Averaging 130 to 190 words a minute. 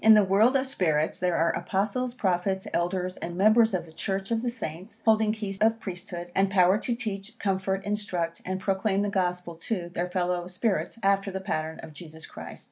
No: average, 200 wpm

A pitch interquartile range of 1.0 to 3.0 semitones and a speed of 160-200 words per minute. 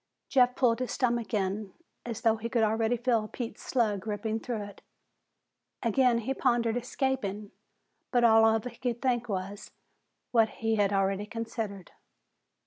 No: narrow, 2.4 semitones; average, 150 wpm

